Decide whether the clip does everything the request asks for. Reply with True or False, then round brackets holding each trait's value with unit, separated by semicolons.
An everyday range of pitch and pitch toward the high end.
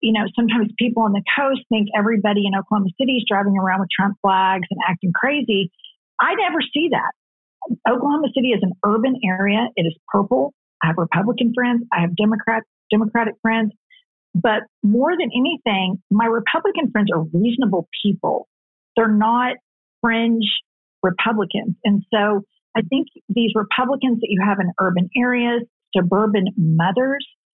True (3.6 semitones; 220 Hz)